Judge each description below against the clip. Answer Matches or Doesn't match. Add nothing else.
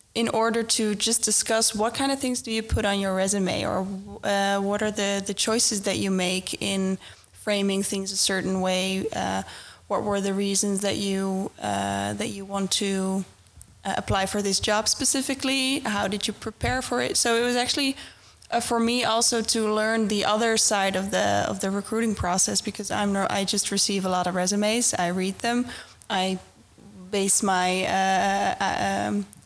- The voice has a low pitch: Doesn't match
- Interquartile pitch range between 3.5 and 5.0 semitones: Doesn't match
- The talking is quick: Doesn't match